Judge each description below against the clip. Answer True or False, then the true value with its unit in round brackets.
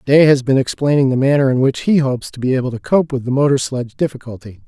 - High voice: False (135 Hz)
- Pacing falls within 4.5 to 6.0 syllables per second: False (6.6 syllables/s)